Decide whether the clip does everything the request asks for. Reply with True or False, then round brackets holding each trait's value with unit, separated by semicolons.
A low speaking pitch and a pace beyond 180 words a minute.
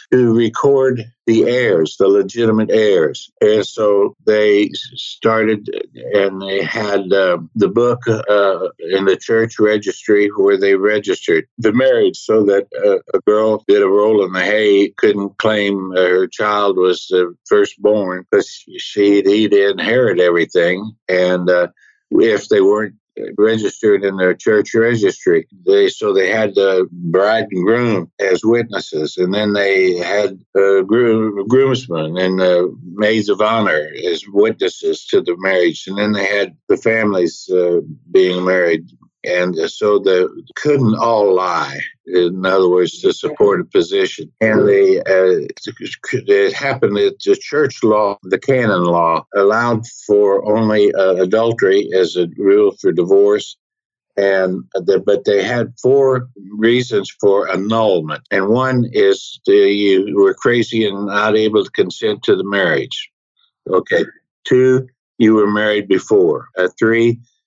False (120 Hz; 145 wpm)